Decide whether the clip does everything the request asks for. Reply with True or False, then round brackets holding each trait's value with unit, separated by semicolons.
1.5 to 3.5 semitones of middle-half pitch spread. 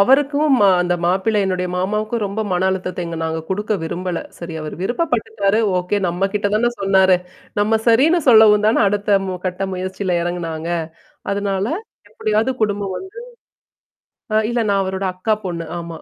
True (3.1 semitones)